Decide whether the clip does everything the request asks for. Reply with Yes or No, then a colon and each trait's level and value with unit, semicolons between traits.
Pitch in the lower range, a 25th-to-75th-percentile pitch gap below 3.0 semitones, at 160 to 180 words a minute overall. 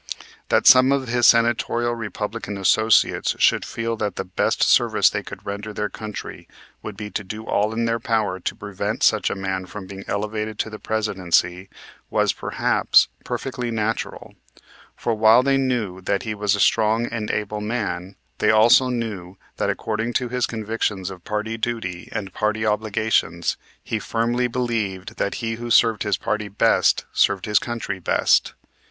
Yes: low, 110 Hz; narrow, 2.4 semitones; average, 170 wpm